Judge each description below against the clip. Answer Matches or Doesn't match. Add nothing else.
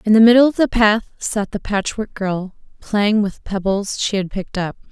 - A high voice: Matches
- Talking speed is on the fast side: Matches